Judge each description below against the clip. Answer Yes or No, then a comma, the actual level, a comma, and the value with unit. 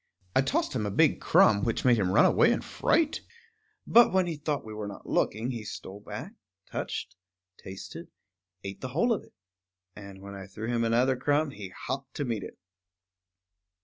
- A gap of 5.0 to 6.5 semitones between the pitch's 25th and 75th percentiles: Yes, average, 5.3 semitones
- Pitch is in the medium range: No, low, 115 Hz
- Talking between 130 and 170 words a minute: No, average, 185 wpm